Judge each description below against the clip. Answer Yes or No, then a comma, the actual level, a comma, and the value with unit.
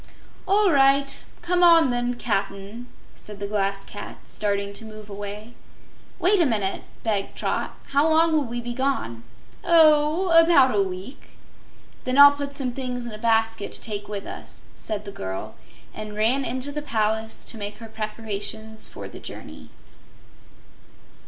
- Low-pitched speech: No, high, 230 Hz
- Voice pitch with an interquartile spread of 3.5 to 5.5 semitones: Yes, average, 5.1 semitones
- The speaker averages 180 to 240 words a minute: No, average, 160 wpm